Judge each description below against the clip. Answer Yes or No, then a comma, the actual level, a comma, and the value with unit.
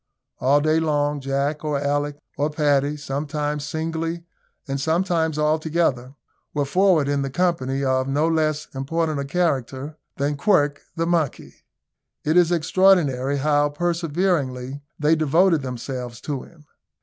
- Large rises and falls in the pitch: No, average, 2.8 semitones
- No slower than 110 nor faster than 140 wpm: Yes, slow, 135 wpm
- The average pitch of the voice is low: No, medium, 150 Hz